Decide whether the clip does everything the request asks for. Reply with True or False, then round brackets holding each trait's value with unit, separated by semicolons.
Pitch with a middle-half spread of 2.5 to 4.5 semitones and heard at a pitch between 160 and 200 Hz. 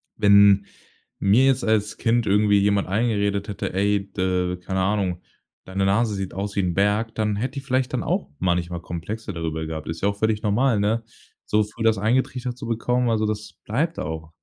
False (2.8 semitones; 105 Hz)